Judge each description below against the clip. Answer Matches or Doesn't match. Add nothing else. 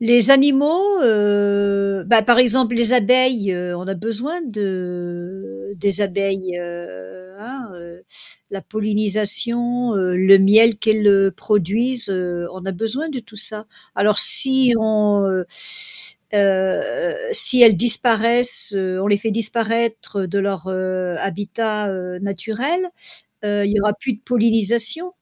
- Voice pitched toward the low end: Doesn't match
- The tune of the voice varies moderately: Matches